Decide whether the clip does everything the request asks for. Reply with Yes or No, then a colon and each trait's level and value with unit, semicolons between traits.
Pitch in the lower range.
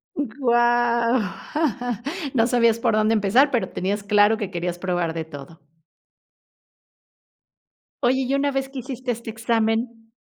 No: high, 230 Hz